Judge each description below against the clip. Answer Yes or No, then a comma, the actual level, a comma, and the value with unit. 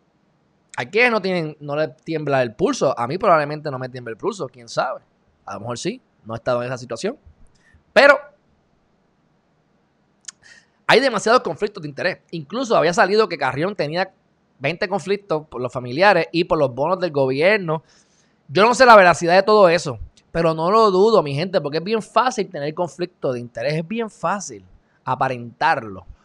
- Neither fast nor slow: Yes, average, 180 wpm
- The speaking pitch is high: No, medium, 165 Hz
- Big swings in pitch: Yes, wide, 7.2 semitones